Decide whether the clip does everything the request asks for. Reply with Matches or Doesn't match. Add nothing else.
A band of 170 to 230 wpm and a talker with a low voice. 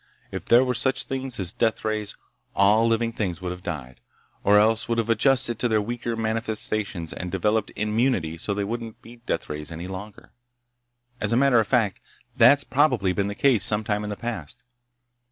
Matches